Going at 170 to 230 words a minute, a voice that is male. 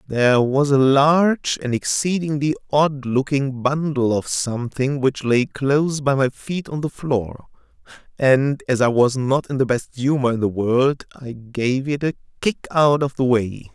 Yes: average, 180 wpm; male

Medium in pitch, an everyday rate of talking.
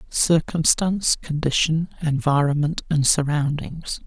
No: medium, 155 Hz; slow, 75 wpm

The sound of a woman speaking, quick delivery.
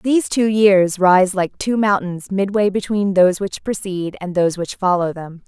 No: female; average, 185 wpm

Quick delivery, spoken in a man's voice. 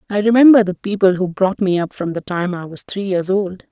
No: fast, 260 wpm; female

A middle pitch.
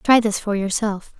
No: high, 210 Hz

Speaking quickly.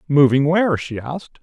No: average, 170 wpm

